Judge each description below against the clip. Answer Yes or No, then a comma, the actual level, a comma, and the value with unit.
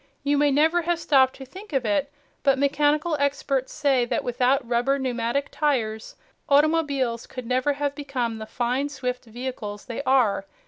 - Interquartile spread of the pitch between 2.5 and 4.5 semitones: Yes, average, 2.8 semitones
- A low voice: No, very high, 270 Hz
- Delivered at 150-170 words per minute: Yes, average, 165 wpm